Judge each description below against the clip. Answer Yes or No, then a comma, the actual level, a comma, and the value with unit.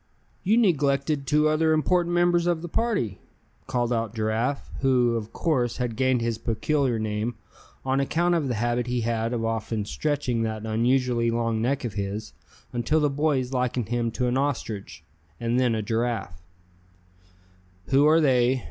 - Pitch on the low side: Yes, low, 125 Hz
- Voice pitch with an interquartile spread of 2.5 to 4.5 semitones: Yes, average, 4.1 semitones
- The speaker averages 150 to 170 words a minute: Yes, average, 165 wpm